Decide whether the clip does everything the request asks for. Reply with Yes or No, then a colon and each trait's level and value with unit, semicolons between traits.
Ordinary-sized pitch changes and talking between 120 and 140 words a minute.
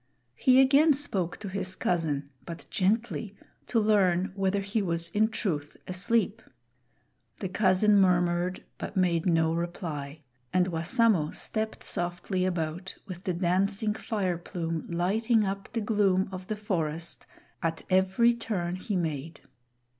Yes: average, 3.5 semitones; slow, 135 wpm